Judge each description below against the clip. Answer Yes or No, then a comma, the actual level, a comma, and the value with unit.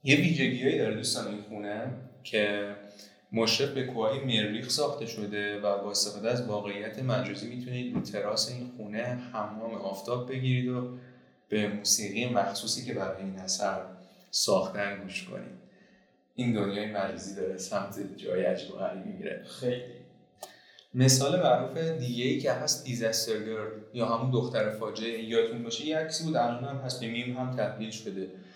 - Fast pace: No, average, 145 wpm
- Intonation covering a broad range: No, average, 3.3 semitones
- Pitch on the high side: No, low, 115 Hz